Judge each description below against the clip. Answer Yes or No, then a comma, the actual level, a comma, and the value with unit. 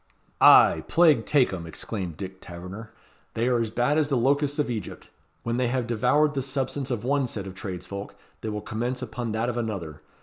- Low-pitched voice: Yes, low, 120 Hz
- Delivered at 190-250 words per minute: Yes, average, 200 wpm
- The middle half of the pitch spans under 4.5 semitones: No, average, 4.8 semitones